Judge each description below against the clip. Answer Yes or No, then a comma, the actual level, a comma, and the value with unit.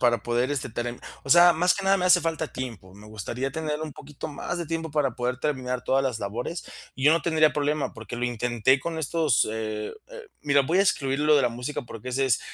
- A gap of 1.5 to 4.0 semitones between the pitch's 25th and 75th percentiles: No, average, 4.5 semitones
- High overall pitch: No, low, 135 Hz